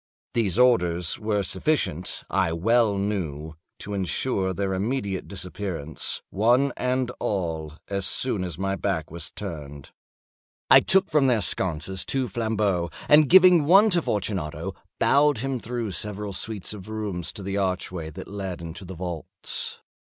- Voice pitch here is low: Yes, low, 100 Hz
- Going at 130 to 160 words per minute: Yes, average, 145 wpm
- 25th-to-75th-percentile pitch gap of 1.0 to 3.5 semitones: No, average, 5.0 semitones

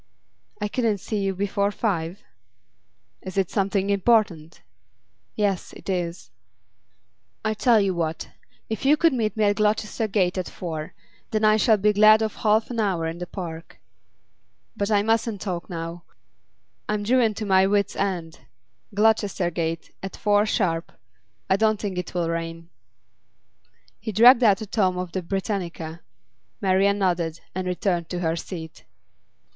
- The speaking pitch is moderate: No, high, 195 Hz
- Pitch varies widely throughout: No, average, 3.5 semitones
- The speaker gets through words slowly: No, average, 150 wpm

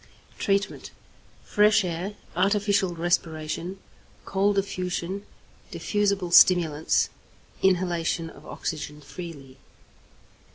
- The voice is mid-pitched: Yes, medium, 180 Hz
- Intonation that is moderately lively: Yes, average, 3.3 semitones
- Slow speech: Yes, slow, 75 wpm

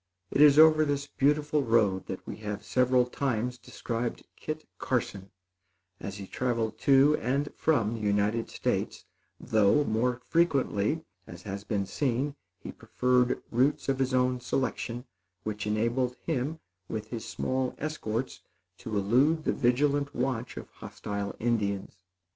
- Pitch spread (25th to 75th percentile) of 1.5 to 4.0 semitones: No, average, 4.5 semitones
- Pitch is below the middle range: Yes, low, 125 Hz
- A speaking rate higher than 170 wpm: No, average, 140 wpm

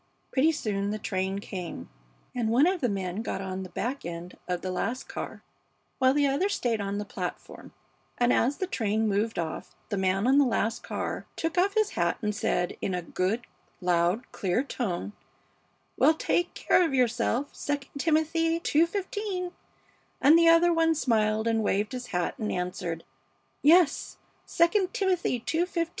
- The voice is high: Yes, high, 240 Hz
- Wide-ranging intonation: Yes, wide, 8.7 semitones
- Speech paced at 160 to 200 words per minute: Yes, average, 170 wpm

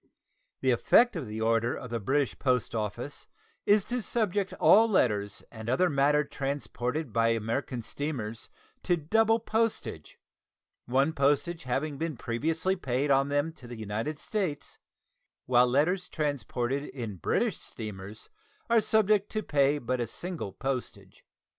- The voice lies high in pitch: No, medium, 140 Hz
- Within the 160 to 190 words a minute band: No, average, 140 wpm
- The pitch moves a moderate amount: No, wide, 5.9 semitones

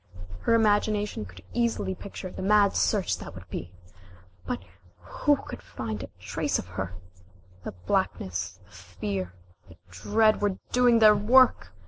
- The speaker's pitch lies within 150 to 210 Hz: Yes, high, 190 Hz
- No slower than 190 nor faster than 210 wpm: No, average, 150 wpm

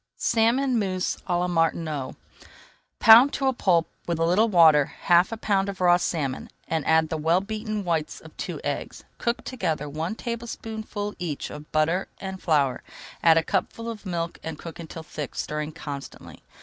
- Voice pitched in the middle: Yes, medium, 175 Hz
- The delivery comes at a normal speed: Yes, average, 175 wpm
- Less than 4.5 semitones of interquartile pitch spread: No, average, 5.0 semitones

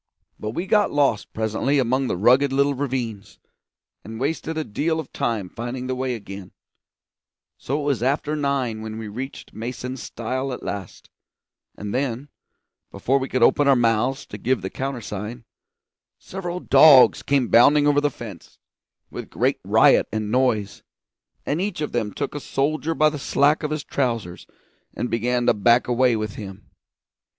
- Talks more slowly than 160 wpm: No, average, 165 wpm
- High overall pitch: No, low, 130 Hz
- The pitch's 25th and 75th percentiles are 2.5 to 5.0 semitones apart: Yes, average, 4.1 semitones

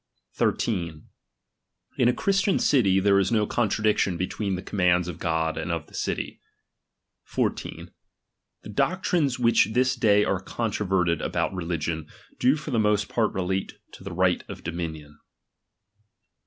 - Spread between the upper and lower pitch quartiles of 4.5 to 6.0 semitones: Yes, average, 5.2 semitones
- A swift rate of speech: No, average, 150 wpm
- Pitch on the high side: No, low, 100 Hz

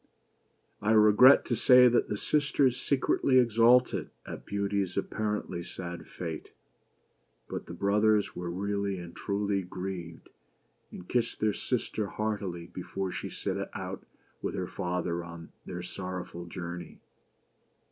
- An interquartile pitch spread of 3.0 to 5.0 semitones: Yes, average, 3.5 semitones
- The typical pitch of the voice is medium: No, low, 100 Hz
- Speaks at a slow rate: Yes, slow, 125 wpm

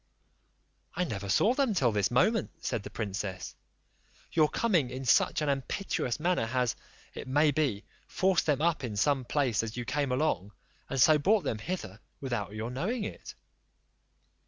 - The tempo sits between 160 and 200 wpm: Yes, average, 165 wpm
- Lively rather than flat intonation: Yes, wide, 6.0 semitones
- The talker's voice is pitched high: No, low, 135 Hz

